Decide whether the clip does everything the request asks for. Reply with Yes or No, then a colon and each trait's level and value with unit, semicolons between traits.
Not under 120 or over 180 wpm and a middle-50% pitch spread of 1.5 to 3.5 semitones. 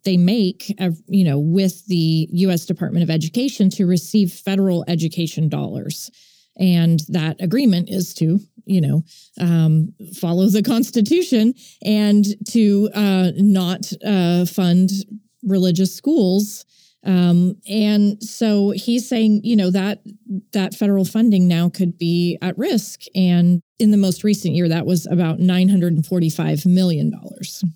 Yes: slow, 135 wpm; average, 2.9 semitones